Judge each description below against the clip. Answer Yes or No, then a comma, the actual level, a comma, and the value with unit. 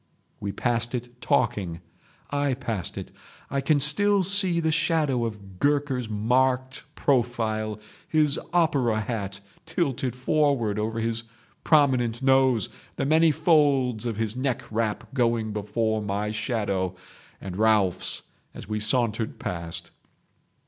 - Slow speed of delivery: Yes, slow, 125 wpm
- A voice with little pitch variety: No, average, 4.5 semitones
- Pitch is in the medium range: No, low, 120 Hz